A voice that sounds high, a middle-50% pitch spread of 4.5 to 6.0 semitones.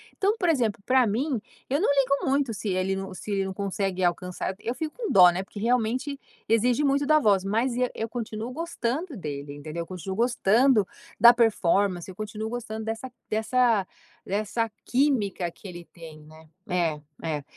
Yes: high, 220 Hz; average, 5.2 semitones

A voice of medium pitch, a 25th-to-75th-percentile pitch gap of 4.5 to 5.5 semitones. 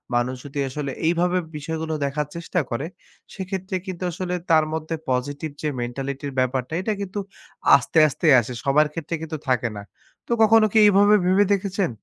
Yes: medium, 160 Hz; average, 5.1 semitones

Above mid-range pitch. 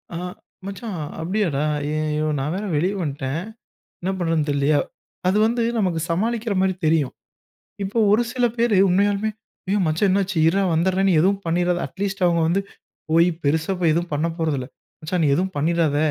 No: medium, 175 Hz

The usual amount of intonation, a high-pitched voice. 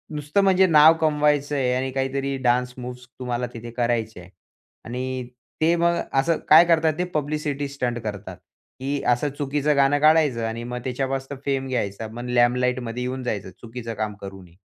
No: average, 3.4 semitones; low, 130 Hz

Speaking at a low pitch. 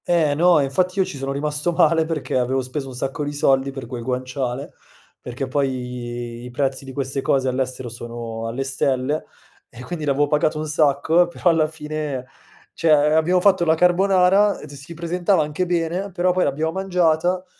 No: medium, 145 Hz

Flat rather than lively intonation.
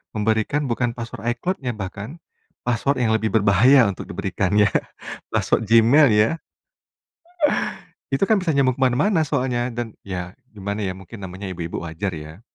No: average, 4.4 semitones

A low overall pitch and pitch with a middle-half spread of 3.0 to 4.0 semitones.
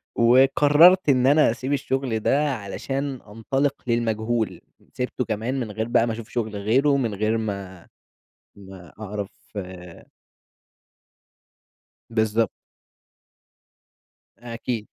Yes: low, 115 Hz; average, 3.6 semitones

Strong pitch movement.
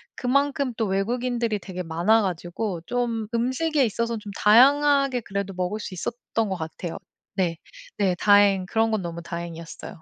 No: average, 4.9 semitones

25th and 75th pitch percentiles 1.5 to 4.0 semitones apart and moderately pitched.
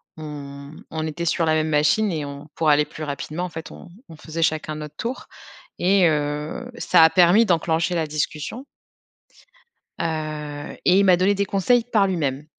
Yes: average, 3.3 semitones; medium, 160 Hz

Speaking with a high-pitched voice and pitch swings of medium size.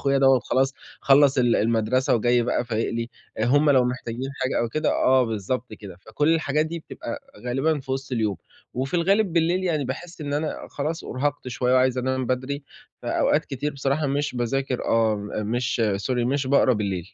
No: low, 130 Hz; average, 3.2 semitones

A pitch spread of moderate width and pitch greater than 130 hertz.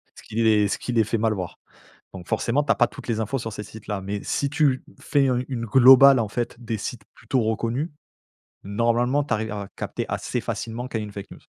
No: average, 3.4 semitones; low, 115 Hz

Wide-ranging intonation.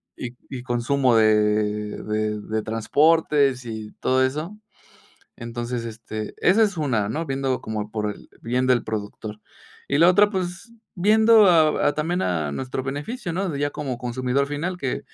Yes: wide, 6.5 semitones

